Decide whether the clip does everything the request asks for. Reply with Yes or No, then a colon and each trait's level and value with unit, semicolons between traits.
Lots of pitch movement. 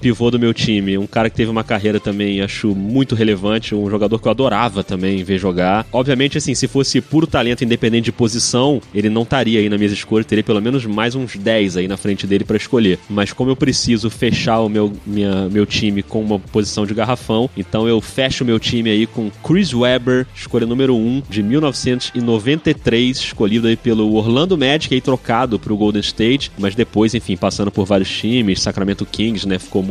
No: average, 3.3 semitones